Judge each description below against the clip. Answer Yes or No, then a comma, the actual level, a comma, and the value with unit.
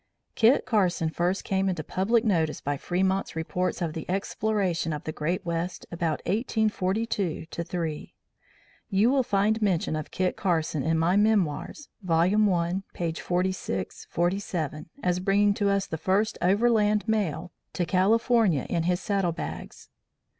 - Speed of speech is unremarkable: Yes, average, 145 wpm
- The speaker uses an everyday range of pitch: Yes, average, 3.6 semitones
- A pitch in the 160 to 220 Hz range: Yes, medium, 185 Hz